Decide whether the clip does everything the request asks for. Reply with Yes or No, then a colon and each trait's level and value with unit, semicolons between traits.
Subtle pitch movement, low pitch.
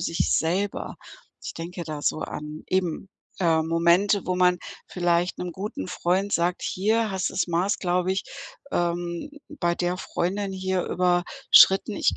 No: narrow, 1.8 semitones; medium, 180 Hz